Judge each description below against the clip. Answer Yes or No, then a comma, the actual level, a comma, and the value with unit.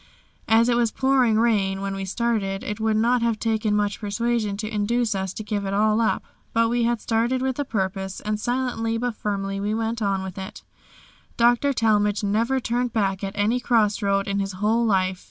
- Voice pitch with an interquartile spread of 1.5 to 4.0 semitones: Yes, average, 2.8 semitones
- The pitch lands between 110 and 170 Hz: No, high, 215 Hz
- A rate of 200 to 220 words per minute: Yes, fast, 205 wpm